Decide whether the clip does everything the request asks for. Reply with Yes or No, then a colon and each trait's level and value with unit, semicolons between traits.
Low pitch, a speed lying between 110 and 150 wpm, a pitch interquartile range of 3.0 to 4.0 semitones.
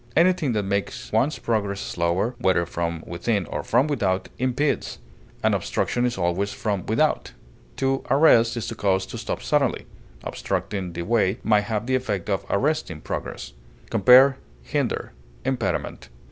No: low, 105 Hz; average, 145 wpm; average, 5.3 semitones